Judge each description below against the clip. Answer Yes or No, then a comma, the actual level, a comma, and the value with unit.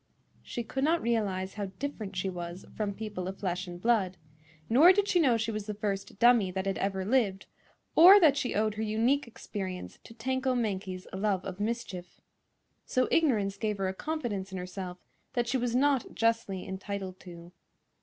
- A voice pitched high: Yes, high, 210 Hz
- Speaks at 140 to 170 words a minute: No, average, 185 wpm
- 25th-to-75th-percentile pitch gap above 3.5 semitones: Yes, average, 4.2 semitones